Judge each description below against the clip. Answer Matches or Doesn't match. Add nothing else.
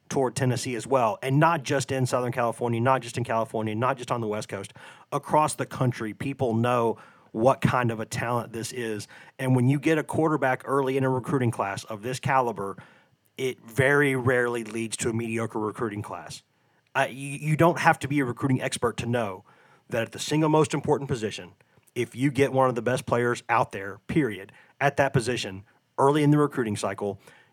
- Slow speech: Doesn't match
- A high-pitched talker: Doesn't match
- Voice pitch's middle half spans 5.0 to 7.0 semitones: Doesn't match